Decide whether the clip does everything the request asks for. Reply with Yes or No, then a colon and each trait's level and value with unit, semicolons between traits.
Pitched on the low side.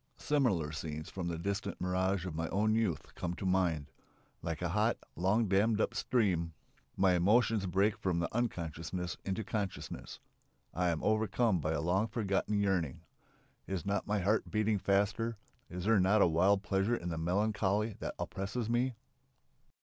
Yes: very low, 95 Hz